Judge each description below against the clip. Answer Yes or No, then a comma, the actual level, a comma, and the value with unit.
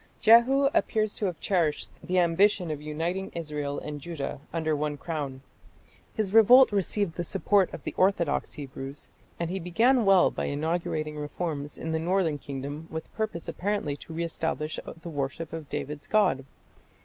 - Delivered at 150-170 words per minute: Yes, average, 160 wpm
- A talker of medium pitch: Yes, medium, 165 Hz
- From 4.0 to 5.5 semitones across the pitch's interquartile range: Yes, average, 4.5 semitones